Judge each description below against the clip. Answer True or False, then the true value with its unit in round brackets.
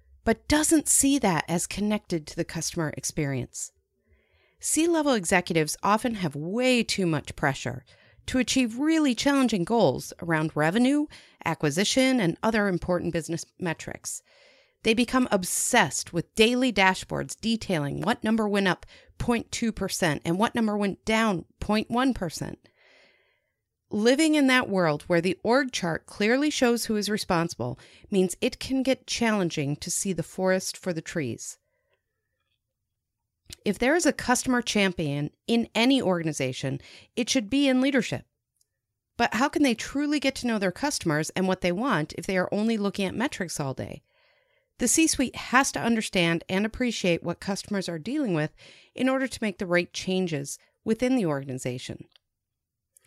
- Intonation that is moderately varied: False (7.2 semitones)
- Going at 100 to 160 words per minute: True (155 wpm)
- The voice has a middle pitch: False (195 Hz)